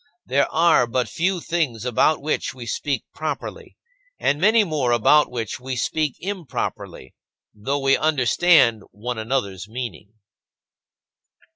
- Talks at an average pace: No, slow, 125 wpm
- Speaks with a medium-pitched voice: No, low, 130 Hz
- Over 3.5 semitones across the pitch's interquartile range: Yes, average, 5.1 semitones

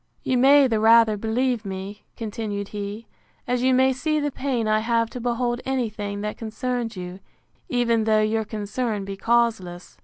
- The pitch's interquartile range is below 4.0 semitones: Yes, average, 2.9 semitones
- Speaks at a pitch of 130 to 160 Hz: No, high, 225 Hz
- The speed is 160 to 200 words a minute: Yes, average, 175 wpm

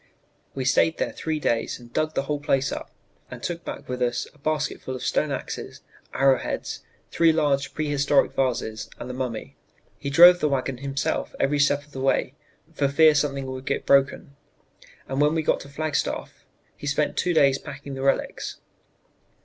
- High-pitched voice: No, medium, 140 Hz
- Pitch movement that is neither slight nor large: No, narrow, 2.1 semitones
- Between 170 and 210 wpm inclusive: Yes, average, 185 wpm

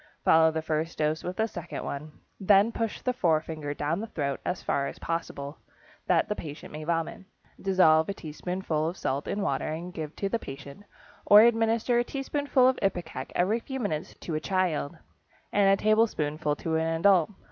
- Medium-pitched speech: Yes, medium, 170 Hz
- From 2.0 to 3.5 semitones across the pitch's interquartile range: No, average, 4.9 semitones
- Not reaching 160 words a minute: No, average, 185 wpm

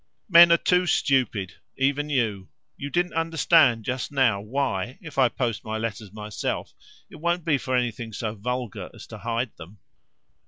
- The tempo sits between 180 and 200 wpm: No, average, 165 wpm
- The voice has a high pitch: No, low, 125 Hz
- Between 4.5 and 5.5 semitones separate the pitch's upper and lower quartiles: Yes, average, 5.1 semitones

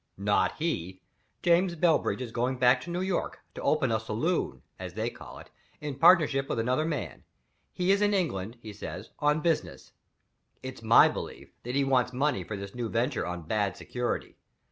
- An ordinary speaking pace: Yes, average, 180 wpm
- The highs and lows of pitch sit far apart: Yes, wide, 6.4 semitones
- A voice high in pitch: No, low, 130 Hz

